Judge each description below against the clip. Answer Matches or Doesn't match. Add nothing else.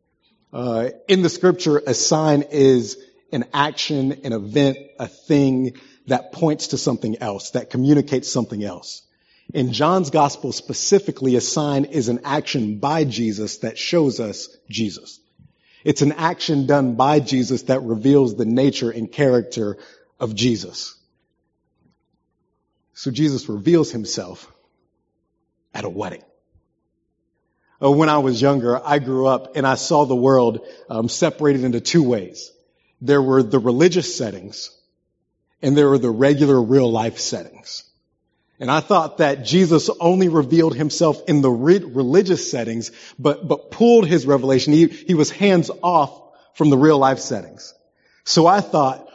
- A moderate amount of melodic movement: Matches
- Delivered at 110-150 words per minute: Matches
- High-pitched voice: Doesn't match